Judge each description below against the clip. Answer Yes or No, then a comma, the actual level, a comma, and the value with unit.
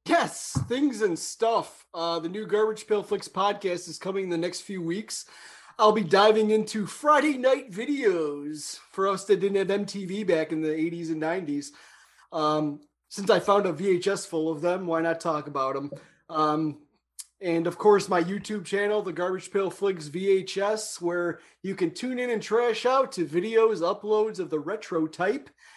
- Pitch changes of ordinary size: Yes, average, 4.4 semitones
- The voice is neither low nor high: No, high, 195 Hz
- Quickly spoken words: No, average, 180 wpm